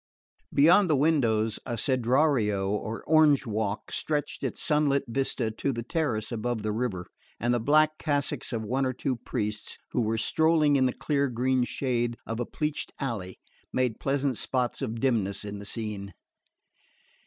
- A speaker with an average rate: Yes, average, 165 wpm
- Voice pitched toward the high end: No, low, 125 Hz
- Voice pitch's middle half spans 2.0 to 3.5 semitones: No, average, 4.3 semitones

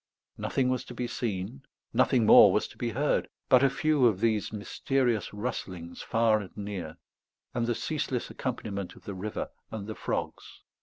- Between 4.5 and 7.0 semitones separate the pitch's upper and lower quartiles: No, average, 3.8 semitones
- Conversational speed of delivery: Yes, average, 170 wpm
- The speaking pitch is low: Yes, low, 110 Hz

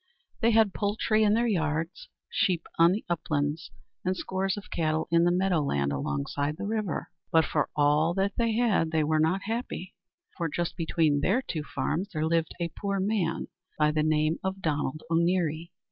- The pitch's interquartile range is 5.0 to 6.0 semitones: No, average, 3.8 semitones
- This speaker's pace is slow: No, average, 170 wpm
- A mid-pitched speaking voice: Yes, medium, 170 Hz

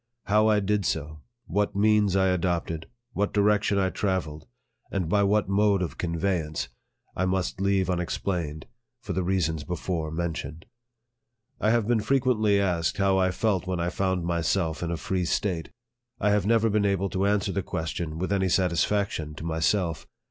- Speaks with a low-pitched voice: Yes, very low, 95 Hz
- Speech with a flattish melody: No, average, 3.2 semitones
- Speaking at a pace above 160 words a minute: Yes, average, 170 wpm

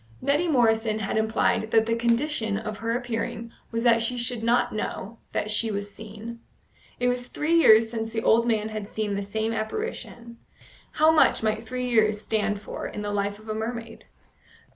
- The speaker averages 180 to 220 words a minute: Yes, average, 185 wpm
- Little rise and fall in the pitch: Yes, narrow, 1.7 semitones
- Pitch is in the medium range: No, high, 225 Hz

